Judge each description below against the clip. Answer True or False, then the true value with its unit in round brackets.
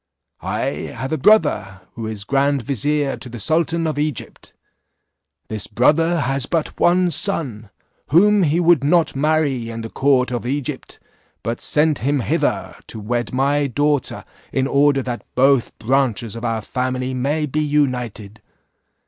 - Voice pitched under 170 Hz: True (135 Hz)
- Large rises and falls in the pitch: False (3.9 semitones)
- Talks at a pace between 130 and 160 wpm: True (150 wpm)